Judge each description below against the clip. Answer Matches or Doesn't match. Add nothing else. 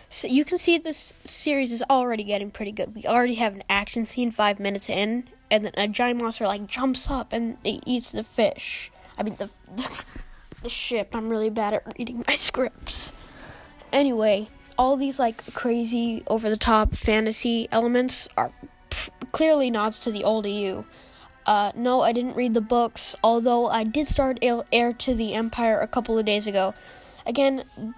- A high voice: Matches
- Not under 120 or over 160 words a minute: Doesn't match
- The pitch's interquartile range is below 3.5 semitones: Matches